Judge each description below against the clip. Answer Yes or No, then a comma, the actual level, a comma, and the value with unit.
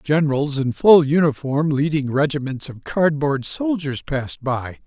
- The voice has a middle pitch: Yes, medium, 145 Hz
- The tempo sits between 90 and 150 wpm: Yes, slow, 135 wpm